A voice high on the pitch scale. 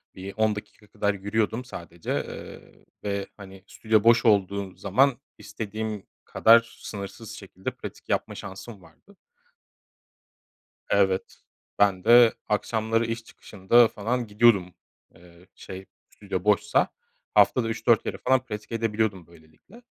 No: low, 105 Hz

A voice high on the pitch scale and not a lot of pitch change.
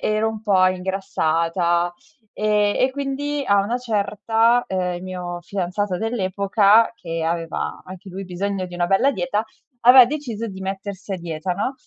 No: high, 200 Hz; average, 3.6 semitones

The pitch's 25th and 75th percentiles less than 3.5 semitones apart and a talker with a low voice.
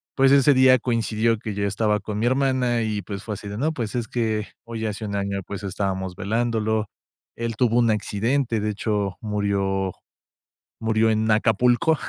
Yes: average, 2.7 semitones; low, 110 Hz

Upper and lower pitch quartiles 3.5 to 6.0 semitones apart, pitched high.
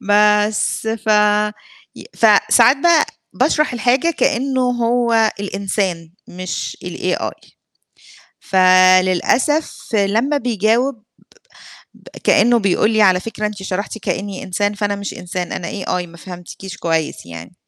Yes: average, 4.2 semitones; high, 205 Hz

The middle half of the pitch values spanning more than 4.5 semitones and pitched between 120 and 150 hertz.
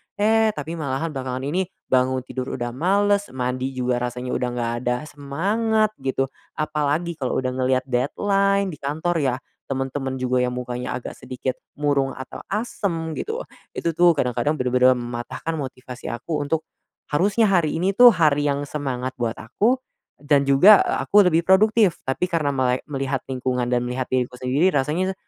Yes: average, 5.2 semitones; medium, 140 Hz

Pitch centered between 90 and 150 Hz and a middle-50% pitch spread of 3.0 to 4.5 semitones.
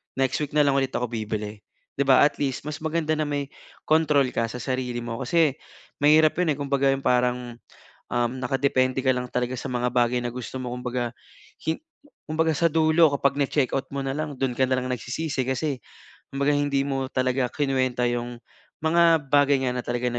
No: low, 135 Hz; narrow, 2.6 semitones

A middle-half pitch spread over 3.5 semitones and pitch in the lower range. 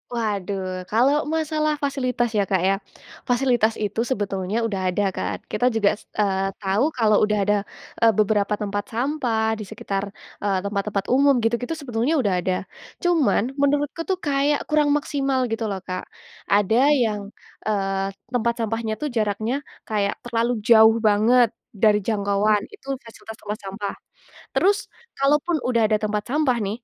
No: average, 4.1 semitones; high, 220 Hz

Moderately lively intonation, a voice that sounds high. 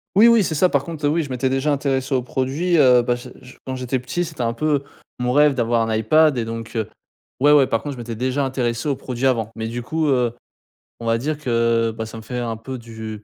No: average, 3.7 semitones; low, 130 Hz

